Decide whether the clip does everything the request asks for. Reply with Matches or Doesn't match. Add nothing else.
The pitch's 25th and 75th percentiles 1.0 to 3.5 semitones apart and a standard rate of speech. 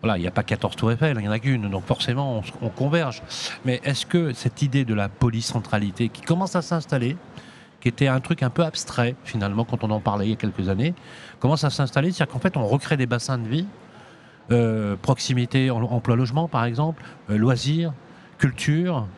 Doesn't match